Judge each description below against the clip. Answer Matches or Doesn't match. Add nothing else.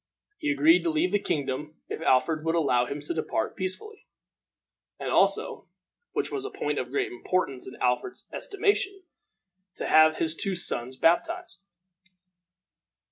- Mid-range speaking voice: Matches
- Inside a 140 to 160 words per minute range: Matches